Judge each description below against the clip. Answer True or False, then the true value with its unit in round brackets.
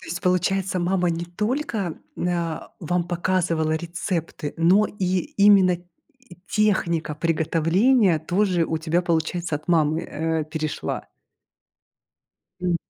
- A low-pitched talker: False (175 Hz)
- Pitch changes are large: False (2.5 semitones)